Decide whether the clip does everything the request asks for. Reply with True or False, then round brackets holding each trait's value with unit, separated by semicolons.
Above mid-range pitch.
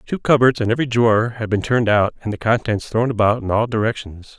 False (115 Hz)